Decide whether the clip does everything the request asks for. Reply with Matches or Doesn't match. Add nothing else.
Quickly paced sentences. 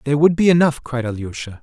Matches